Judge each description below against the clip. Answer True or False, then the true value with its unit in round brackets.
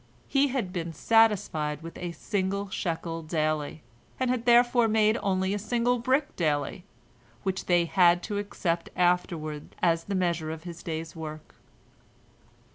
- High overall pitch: False (180 Hz)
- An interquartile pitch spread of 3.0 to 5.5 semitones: True (4.6 semitones)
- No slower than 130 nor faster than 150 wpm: True (145 wpm)